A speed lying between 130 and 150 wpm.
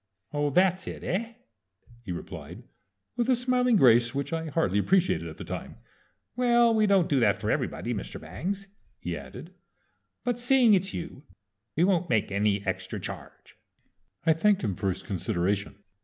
No: average, 165 wpm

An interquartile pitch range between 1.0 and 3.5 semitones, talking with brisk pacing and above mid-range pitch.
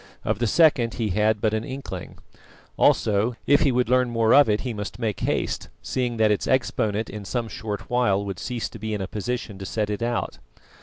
No: average, 2.8 semitones; fast, 215 wpm; low, 110 Hz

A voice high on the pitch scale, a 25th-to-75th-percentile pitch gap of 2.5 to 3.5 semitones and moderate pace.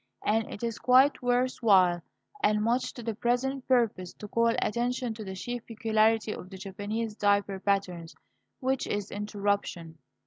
Yes: high, 215 Hz; average, 3.2 semitones; average, 160 wpm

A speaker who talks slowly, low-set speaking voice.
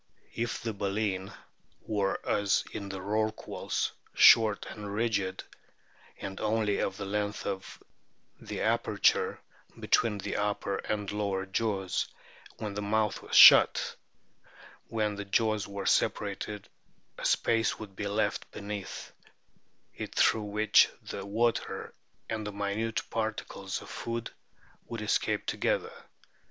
Yes: slow, 125 wpm; low, 105 Hz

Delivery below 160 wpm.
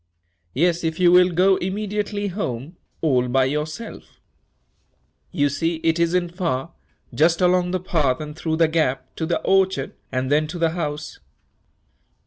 Yes: average, 150 wpm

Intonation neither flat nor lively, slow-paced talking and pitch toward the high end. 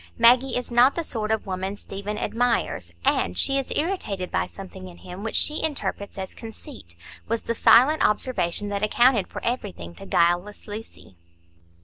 No: average, 4.6 semitones; average, 165 wpm; high, 210 Hz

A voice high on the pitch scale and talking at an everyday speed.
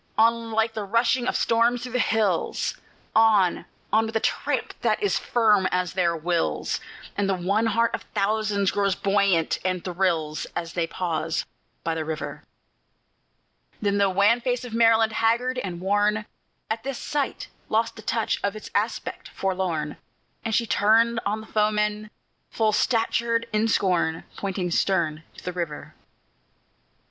Yes: high, 210 Hz; average, 155 wpm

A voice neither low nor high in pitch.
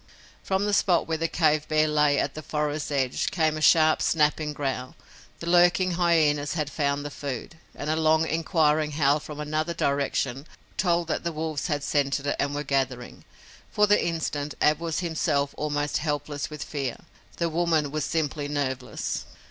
Yes: medium, 150 Hz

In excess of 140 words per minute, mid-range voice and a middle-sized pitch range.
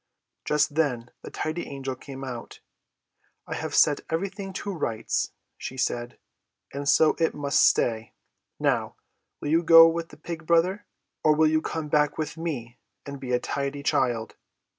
Yes: average, 160 wpm; medium, 150 Hz; average, 3.6 semitones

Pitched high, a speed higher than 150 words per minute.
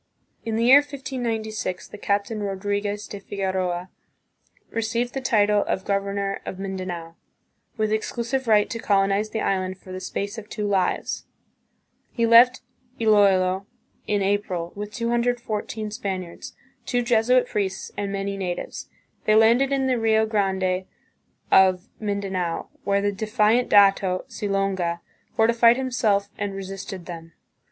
No: high, 205 Hz; slow, 135 wpm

